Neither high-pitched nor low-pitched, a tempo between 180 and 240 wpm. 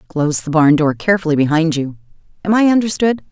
No: medium, 165 Hz; average, 165 wpm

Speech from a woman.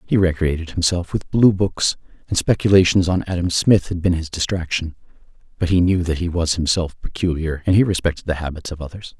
No: male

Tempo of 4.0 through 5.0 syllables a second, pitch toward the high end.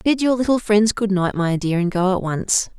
Yes: 4.9 syllables/s; high, 200 Hz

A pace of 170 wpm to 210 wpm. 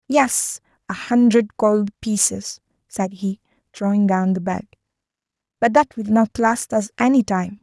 No: average, 150 wpm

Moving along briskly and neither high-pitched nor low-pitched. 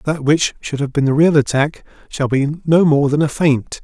Yes: fast, 235 wpm; medium, 145 Hz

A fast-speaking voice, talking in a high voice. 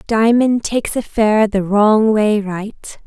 No: average, 155 wpm; high, 215 Hz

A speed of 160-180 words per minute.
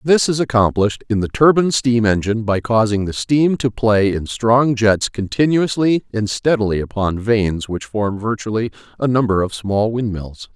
Yes: average, 170 wpm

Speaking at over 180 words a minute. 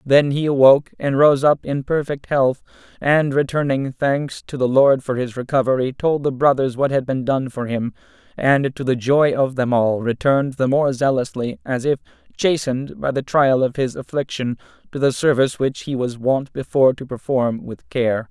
Yes: average, 195 wpm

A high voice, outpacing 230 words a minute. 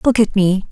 Yes: high, 205 Hz; fast, 250 wpm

